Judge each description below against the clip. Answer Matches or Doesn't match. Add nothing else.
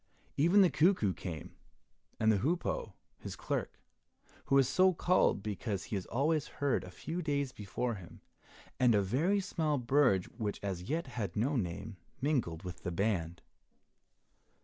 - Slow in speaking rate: Doesn't match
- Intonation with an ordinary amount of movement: Doesn't match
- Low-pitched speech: Matches